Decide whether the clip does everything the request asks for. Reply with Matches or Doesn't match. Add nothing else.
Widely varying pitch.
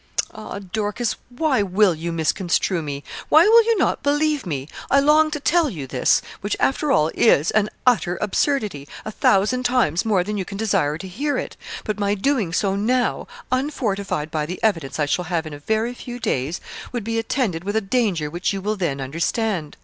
Matches